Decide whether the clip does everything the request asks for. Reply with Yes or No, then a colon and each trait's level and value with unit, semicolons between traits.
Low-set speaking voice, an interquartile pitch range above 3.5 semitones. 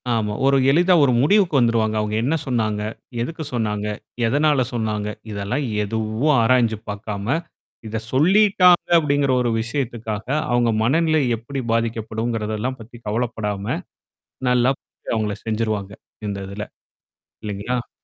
Yes: low, 115 Hz; average, 4.2 semitones